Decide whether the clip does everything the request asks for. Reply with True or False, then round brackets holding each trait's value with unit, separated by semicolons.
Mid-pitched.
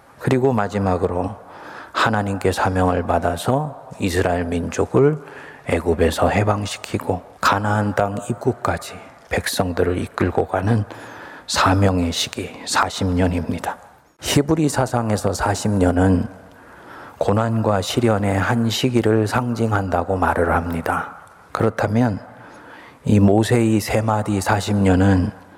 False (100 Hz)